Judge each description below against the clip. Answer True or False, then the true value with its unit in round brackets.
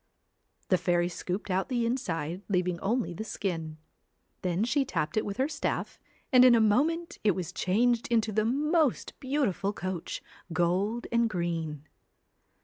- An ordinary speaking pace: True (150 wpm)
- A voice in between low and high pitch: False (205 Hz)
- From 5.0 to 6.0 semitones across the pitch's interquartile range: True (5.6 semitones)